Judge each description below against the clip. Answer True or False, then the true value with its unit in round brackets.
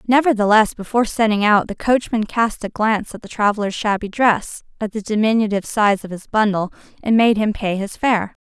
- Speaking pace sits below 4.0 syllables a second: False (5.5 syllables/s)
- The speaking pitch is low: False (215 Hz)